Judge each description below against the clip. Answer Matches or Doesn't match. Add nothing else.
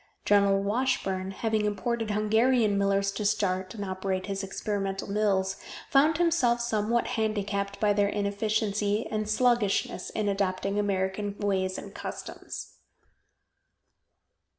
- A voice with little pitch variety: Matches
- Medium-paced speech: Doesn't match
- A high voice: Matches